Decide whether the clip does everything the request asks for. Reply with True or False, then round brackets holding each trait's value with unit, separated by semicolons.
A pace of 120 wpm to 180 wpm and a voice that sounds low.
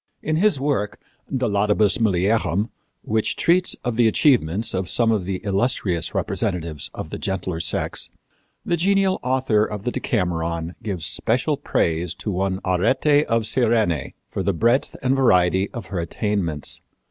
True (150 wpm; 105 Hz)